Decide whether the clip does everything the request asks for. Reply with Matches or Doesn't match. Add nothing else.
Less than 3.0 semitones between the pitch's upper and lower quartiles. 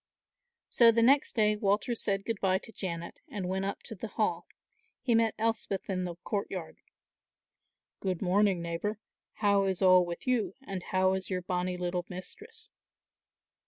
Doesn't match